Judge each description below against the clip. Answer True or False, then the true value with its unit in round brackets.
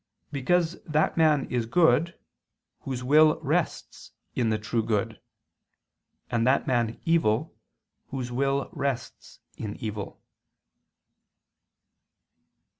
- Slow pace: True (100 wpm)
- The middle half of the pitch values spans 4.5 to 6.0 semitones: True (4.9 semitones)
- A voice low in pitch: True (130 Hz)